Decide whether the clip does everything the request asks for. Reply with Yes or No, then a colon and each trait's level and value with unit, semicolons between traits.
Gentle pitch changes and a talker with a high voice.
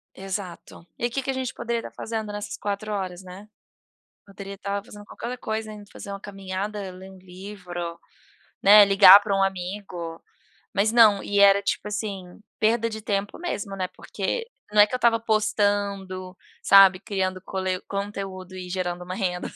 Yes: narrow, 2.0 semitones; high, 200 Hz